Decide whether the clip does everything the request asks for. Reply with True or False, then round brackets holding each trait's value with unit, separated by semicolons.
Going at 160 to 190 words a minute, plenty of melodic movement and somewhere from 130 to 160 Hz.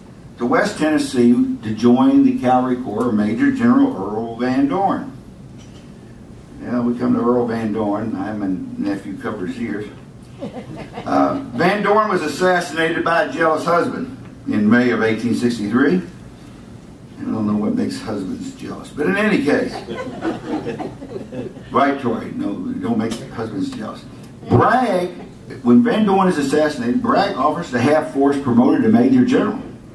False (145 wpm; 8.2 semitones; 140 Hz)